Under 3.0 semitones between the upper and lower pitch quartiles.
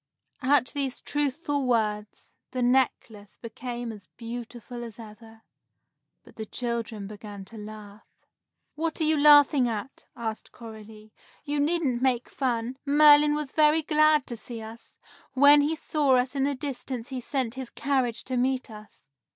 No: average, 4.1 semitones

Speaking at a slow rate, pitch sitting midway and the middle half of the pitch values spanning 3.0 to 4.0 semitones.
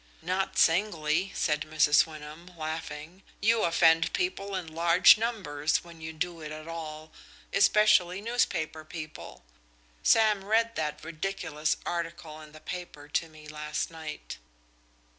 Yes: slow, 130 wpm; medium, 165 Hz; average, 3.3 semitones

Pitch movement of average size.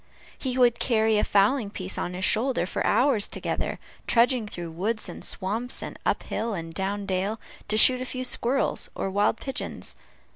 Yes: average, 4.2 semitones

